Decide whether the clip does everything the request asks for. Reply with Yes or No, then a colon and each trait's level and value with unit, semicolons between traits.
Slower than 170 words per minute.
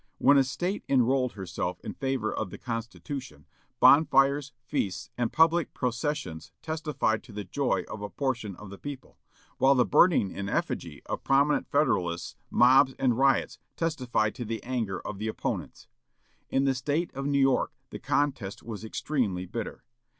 Yes: average, 160 wpm